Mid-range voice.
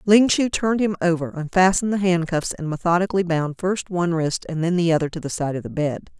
Yes: medium, 175 Hz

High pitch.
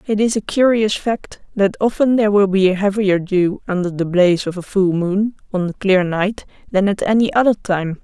Yes: high, 195 Hz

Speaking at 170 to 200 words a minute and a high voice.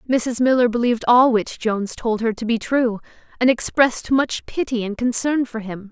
Yes: average, 195 wpm; high, 235 Hz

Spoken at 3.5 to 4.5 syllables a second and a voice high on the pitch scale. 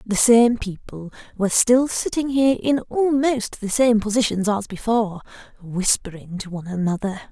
No: 5.1 syllables/s; high, 220 Hz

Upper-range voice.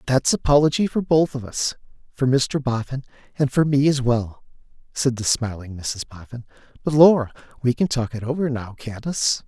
No: low, 130 Hz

